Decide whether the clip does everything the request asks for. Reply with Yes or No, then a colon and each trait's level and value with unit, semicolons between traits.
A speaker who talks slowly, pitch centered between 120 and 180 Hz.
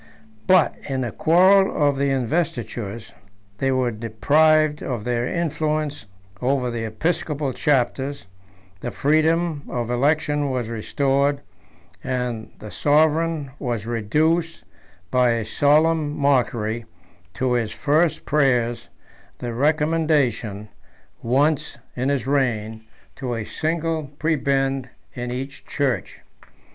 Yes: slow, 110 wpm; low, 135 Hz